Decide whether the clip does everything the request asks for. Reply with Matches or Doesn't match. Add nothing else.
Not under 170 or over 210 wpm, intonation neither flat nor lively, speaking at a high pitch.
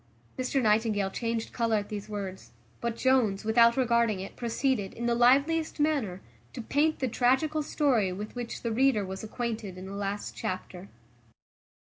Doesn't match